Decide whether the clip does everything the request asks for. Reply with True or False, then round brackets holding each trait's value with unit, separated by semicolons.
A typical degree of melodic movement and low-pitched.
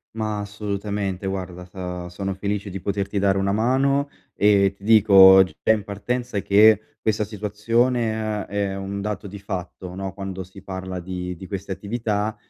False (1.8 semitones; 100 Hz)